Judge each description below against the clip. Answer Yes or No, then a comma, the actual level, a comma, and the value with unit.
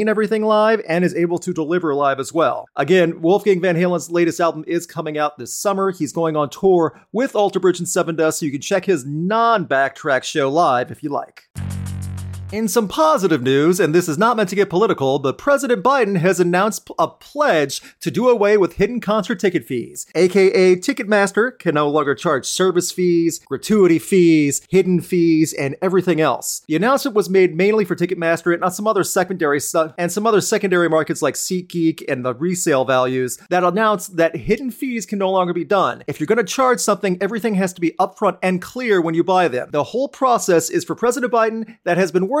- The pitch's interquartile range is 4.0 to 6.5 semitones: Yes, average, 4.3 semitones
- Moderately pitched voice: Yes, medium, 180 Hz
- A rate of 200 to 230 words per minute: Yes, fast, 205 wpm